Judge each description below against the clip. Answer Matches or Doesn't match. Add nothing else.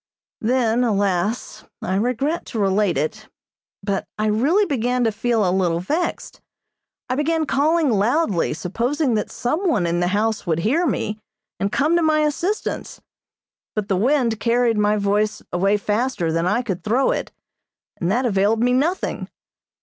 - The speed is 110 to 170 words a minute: Matches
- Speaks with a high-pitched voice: Matches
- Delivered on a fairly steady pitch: Doesn't match